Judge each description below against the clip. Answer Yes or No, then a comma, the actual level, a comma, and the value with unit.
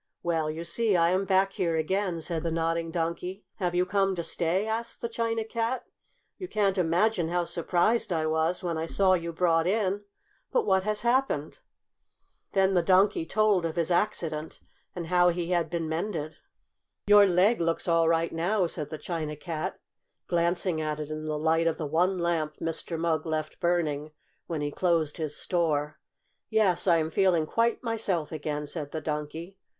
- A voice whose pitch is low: No, medium, 170 Hz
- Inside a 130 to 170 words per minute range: No, average, 180 wpm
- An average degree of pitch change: Yes, average, 3.0 semitones